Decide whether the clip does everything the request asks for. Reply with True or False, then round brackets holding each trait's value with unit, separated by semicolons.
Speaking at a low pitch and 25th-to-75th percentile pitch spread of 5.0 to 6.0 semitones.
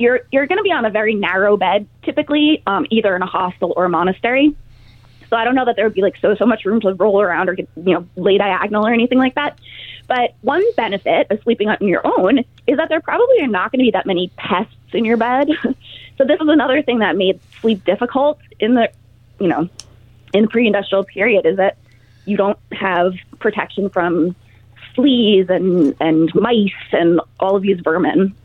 False (205 Hz; 5.5 semitones)